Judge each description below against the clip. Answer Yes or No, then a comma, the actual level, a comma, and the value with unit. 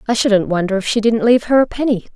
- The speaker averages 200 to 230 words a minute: No, fast, 280 wpm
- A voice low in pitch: No, high, 220 Hz